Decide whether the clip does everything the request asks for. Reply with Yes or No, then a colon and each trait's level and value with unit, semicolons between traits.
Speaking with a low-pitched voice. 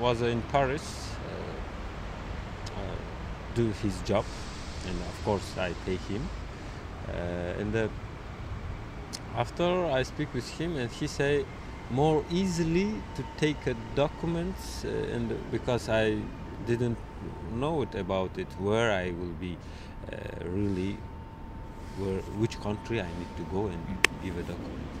Yes: low, 100 Hz